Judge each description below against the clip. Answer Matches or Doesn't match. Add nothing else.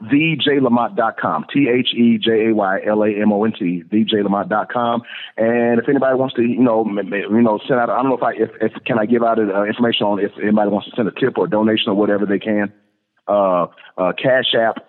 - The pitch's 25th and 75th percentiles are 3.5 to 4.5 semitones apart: Doesn't match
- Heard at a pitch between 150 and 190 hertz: Doesn't match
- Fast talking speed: Matches